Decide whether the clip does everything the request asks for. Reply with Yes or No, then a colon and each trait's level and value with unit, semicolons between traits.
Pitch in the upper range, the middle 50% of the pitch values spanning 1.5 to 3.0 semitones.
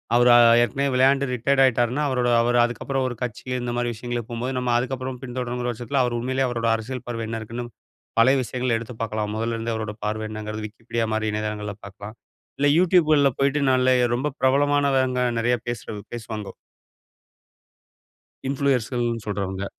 No: low, 120 Hz; narrow, 2.6 semitones